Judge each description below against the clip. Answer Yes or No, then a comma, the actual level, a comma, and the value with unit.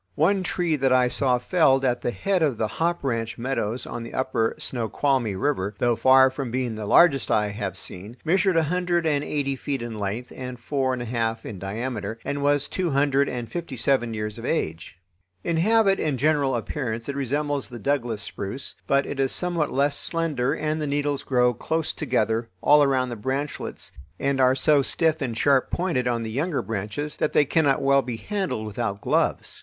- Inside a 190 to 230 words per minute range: Yes, average, 200 wpm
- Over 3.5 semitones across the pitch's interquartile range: Yes, average, 4.0 semitones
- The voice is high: No, low, 135 Hz